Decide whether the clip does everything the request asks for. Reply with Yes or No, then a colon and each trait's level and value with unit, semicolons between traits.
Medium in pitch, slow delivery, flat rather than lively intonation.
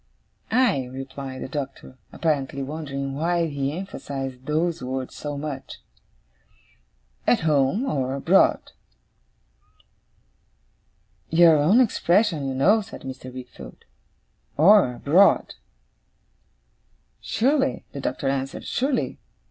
No: medium, 145 Hz; slow, 100 wpm; average, 4.5 semitones